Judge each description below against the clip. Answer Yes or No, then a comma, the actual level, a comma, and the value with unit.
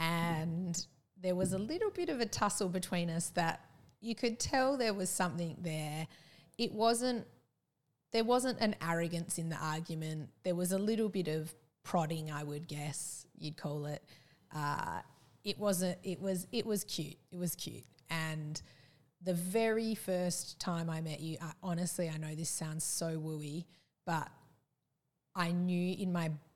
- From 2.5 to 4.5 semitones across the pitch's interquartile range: Yes, average, 3.2 semitones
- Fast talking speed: No, average, 165 wpm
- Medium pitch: Yes, medium, 170 Hz